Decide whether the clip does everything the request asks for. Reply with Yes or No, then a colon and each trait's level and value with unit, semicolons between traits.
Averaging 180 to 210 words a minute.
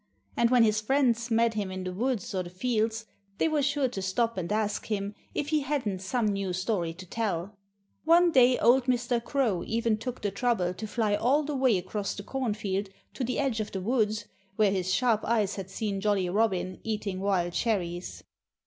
Yes: average, 200 wpm